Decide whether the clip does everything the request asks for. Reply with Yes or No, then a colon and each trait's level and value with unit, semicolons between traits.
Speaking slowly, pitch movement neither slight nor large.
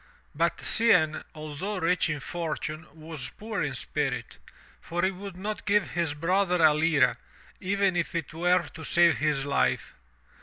No: average, 155 wpm; average, 3.4 semitones